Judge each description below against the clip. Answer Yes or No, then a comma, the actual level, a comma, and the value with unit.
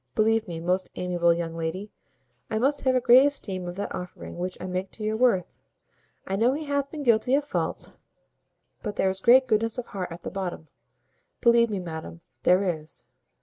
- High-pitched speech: Yes, high, 200 Hz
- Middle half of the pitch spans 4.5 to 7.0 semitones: Yes, average, 5.0 semitones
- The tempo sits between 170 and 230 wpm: Yes, average, 195 wpm